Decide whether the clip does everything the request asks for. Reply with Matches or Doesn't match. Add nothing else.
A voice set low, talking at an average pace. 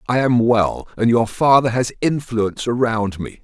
Matches